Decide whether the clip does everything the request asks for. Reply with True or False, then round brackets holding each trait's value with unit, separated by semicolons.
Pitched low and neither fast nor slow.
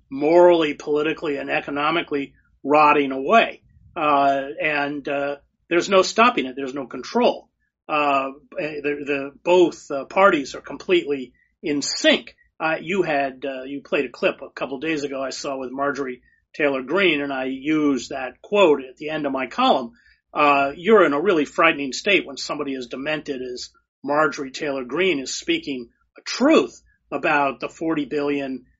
False (145 Hz; 165 wpm)